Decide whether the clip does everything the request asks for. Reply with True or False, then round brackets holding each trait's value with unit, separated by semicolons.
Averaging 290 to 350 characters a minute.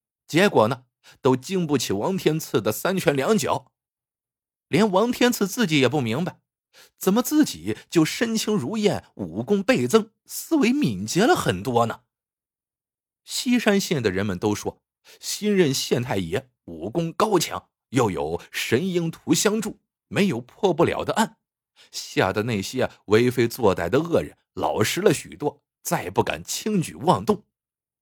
False (215 characters per minute)